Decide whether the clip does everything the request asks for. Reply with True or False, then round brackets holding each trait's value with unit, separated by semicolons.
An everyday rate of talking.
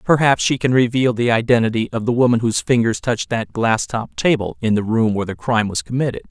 False (230 wpm)